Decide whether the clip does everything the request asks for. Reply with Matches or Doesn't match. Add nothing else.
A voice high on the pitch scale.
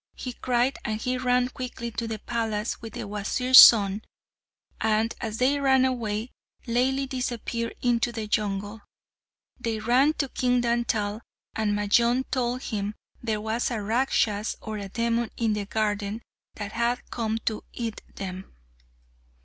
Matches